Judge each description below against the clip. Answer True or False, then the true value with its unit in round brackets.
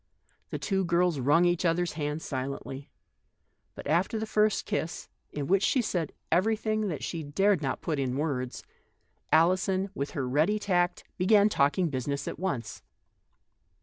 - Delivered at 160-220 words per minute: False (150 wpm)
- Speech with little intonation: False (5.0 semitones)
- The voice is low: False (170 Hz)